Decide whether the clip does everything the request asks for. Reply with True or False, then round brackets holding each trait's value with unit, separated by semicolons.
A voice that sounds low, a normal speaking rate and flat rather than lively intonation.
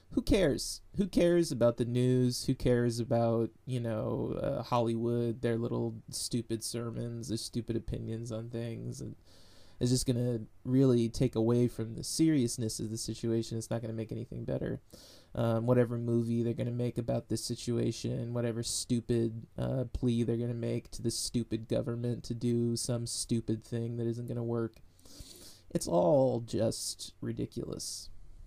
True (115 Hz; 170 wpm; 1.0 semitones)